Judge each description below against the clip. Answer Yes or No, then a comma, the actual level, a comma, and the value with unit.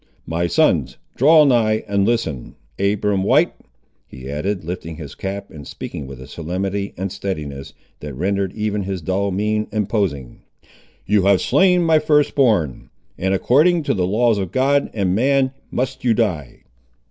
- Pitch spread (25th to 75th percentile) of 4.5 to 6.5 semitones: Yes, average, 5.0 semitones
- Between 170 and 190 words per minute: No, average, 160 wpm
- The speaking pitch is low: Yes, low, 100 Hz